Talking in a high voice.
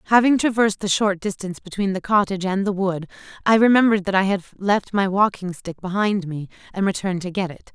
Yes: high, 195 Hz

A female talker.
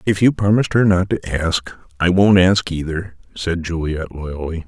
No: male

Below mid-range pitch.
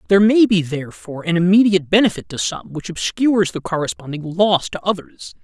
No: medium, 175 Hz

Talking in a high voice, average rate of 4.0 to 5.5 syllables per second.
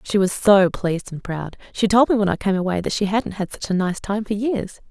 Yes: high, 200 Hz; 5.4 syllables/s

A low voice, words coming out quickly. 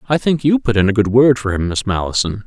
Yes: low, 115 Hz; fast, 290 wpm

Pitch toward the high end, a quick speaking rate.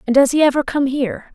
Yes: very high, 270 Hz; fast, 270 wpm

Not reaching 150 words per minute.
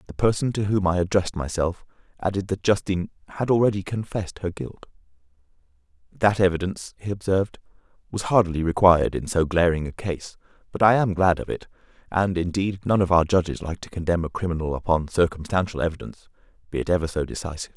No: average, 175 wpm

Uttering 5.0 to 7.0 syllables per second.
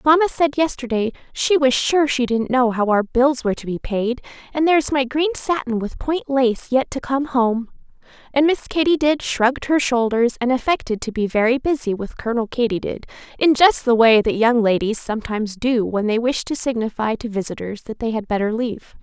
Yes: 5.3 syllables/s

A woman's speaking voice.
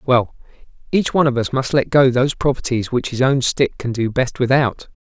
No: male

